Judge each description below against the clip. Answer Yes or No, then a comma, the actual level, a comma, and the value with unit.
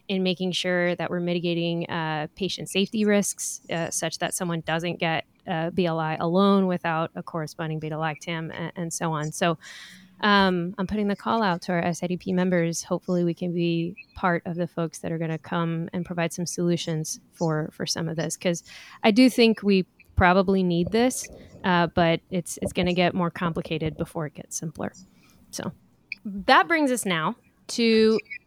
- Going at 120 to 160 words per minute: No, average, 185 wpm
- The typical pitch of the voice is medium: Yes, medium, 175 Hz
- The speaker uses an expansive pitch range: No, narrow, 2.4 semitones